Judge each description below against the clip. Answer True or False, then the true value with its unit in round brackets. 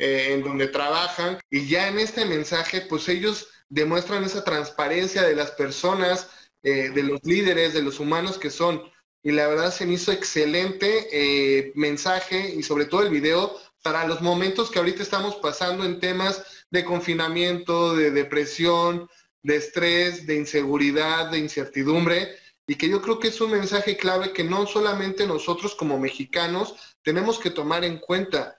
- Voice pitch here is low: False (175 Hz)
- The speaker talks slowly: False (165 wpm)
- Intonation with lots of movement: False (4.0 semitones)